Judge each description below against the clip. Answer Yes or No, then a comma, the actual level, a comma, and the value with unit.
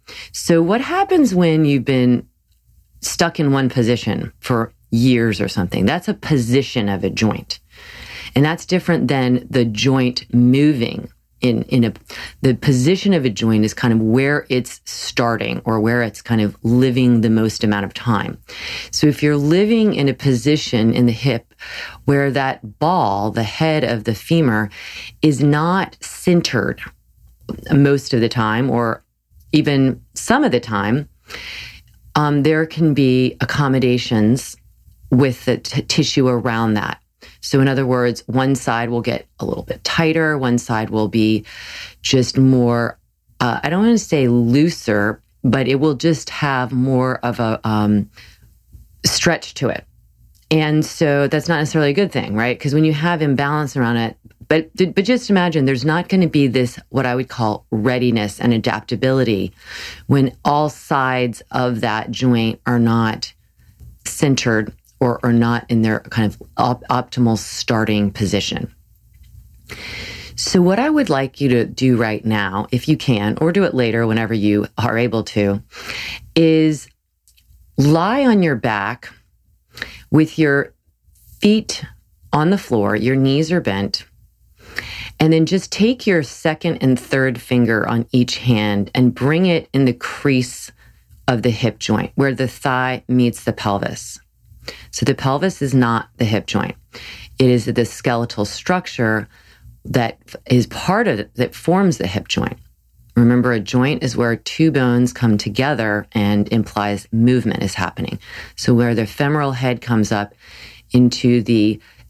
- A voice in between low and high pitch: No, low, 125 Hz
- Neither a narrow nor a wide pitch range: Yes, average, 4.2 semitones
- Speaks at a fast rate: No, average, 155 wpm